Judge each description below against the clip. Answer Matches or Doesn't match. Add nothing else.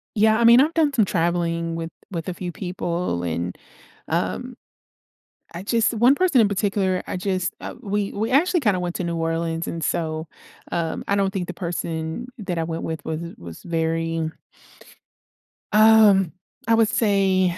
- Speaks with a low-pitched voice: Doesn't match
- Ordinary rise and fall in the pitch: Matches